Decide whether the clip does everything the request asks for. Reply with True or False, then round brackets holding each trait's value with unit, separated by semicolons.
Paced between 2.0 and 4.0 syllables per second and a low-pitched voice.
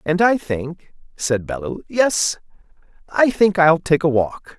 False (3.7 syllables/s; 170 Hz)